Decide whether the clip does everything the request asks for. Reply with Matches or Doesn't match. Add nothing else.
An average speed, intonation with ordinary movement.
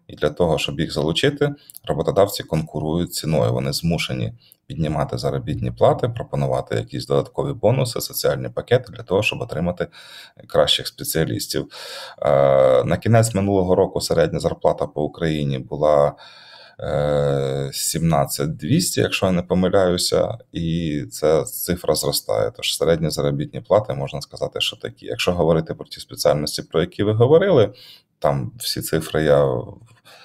Matches